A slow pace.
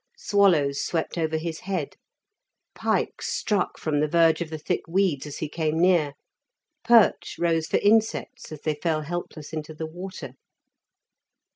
No: average, 150 wpm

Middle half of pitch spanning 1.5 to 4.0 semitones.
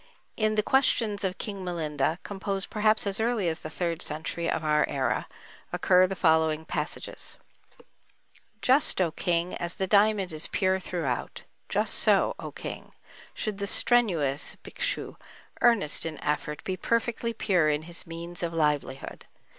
No: average, 4.6 semitones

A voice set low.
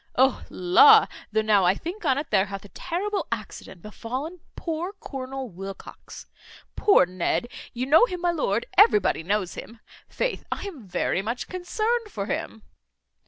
No: very high, 255 Hz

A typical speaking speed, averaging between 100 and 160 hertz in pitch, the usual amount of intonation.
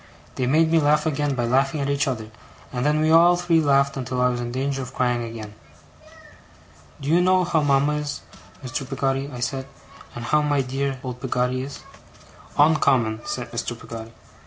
Yes: average, 190 wpm; low, 135 Hz; average, 3.1 semitones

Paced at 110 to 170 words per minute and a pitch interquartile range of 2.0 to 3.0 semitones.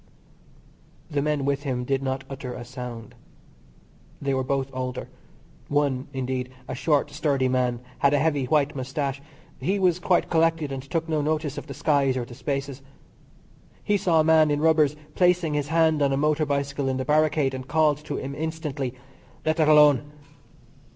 No: average, 180 wpm; average, 2.7 semitones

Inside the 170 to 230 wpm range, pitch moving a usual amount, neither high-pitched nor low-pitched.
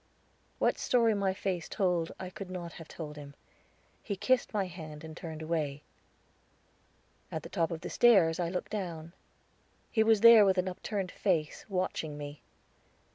No: average, 160 wpm; average, 3.8 semitones; medium, 180 Hz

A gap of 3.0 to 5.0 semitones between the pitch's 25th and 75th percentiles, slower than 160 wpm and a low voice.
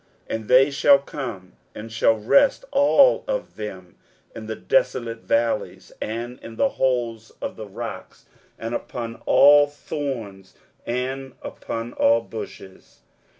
Yes: average, 3.7 semitones; slow, 135 wpm; low, 120 Hz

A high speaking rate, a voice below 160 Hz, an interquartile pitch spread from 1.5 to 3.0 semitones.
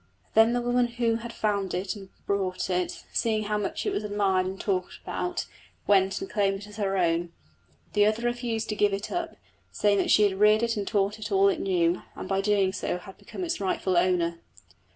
No: fast, 215 wpm; high, 205 Hz; average, 2.7 semitones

